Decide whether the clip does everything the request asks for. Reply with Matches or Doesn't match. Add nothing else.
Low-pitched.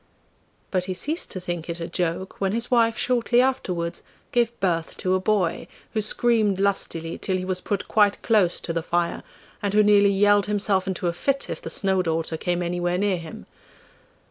Doesn't match